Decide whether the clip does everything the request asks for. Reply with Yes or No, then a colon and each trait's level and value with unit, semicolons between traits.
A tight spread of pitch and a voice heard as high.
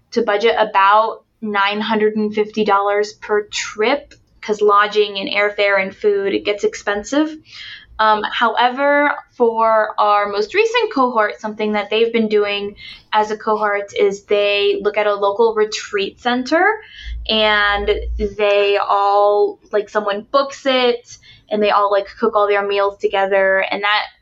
Yes: narrow, 2.1 semitones; high, 210 Hz